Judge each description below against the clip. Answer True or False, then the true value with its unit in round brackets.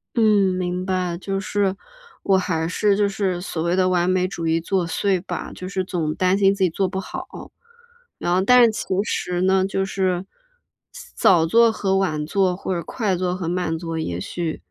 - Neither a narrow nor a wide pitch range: False (1.9 semitones)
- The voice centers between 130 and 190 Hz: True (185 Hz)